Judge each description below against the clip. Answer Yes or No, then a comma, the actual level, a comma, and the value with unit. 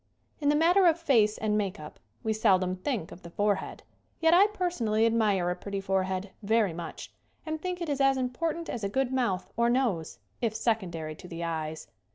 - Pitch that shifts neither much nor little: No, wide, 6.6 semitones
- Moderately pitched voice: No, high, 220 Hz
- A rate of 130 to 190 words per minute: No, fast, 205 wpm